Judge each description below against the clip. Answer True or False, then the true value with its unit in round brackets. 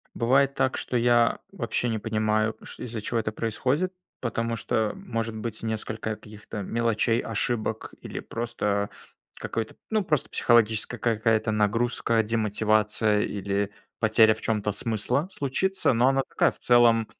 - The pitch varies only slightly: True (1.9 semitones)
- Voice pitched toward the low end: True (115 Hz)